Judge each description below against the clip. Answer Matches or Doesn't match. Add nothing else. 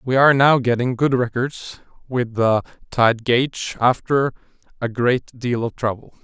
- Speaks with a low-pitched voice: Matches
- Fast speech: Doesn't match